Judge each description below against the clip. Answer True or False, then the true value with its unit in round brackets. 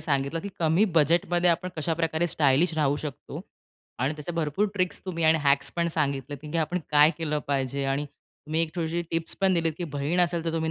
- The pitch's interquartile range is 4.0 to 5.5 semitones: False (2.6 semitones)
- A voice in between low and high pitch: True (160 Hz)